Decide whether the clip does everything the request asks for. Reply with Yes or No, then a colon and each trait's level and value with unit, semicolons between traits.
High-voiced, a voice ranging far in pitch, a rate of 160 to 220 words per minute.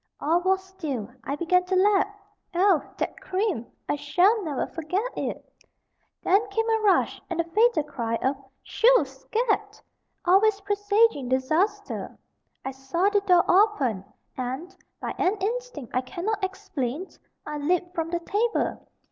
No: very high, 365 Hz; wide, 5.8 semitones; average, 145 wpm